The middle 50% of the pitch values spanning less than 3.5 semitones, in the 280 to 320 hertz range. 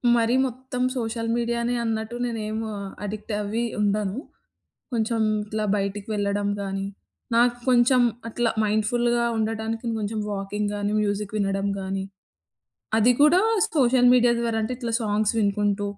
No: narrow, 2.5 semitones; high, 220 Hz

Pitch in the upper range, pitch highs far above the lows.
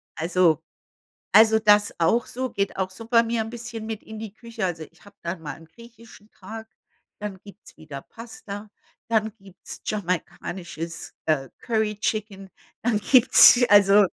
No: high, 210 Hz; average, 3.5 semitones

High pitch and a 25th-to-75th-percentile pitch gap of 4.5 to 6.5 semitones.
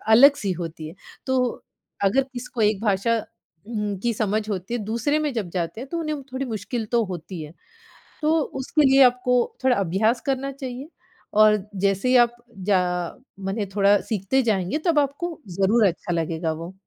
Yes: high, 225 Hz; average, 5.2 semitones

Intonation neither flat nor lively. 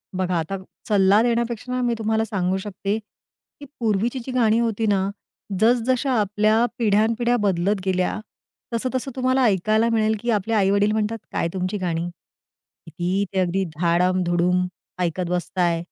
Yes: average, 3.7 semitones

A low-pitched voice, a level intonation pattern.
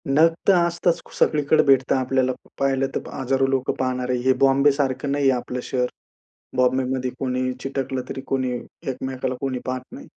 Yes: low, 130 Hz; narrow, 1.3 semitones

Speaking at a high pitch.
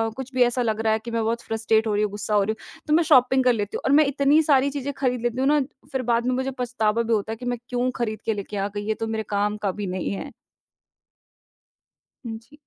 Yes: high, 235 Hz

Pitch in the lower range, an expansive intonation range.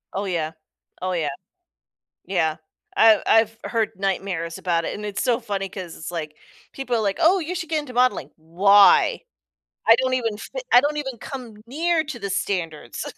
No: high, 210 Hz; wide, 5.8 semitones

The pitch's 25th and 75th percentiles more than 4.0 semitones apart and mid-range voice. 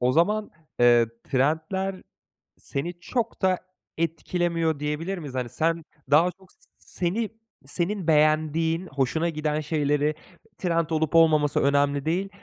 No: average, 2.8 semitones; medium, 160 Hz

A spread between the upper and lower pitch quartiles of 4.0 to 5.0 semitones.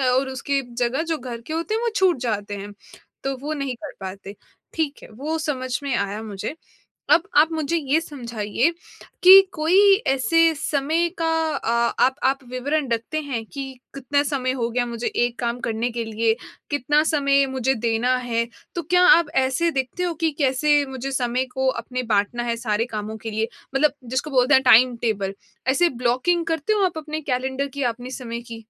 Yes: average, 4.3 semitones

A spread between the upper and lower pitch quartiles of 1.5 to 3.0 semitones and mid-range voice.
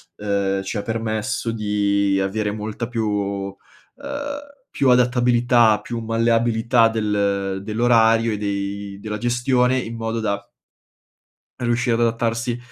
No: narrow, 2.6 semitones; low, 110 Hz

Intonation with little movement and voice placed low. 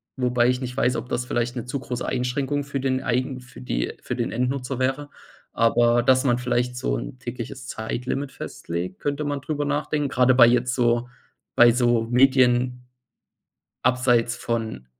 Yes: narrow, 1.7 semitones; low, 125 Hz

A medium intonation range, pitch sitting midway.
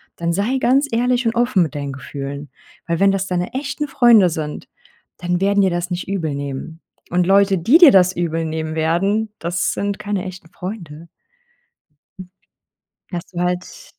Yes: average, 3.9 semitones; medium, 180 Hz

